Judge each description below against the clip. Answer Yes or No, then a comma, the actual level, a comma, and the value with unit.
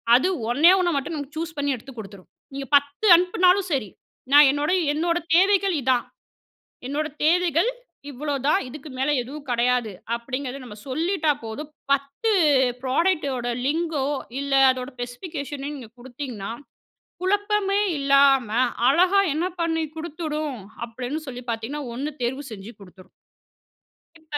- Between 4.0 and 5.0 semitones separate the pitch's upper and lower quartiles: Yes, average, 4.5 semitones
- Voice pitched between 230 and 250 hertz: No, very high, 280 Hz